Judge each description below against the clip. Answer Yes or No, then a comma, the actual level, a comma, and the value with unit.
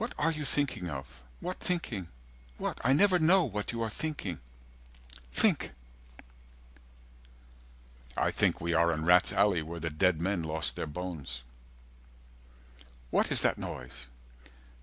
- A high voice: No, very low, 90 Hz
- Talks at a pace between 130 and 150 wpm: Yes, average, 140 wpm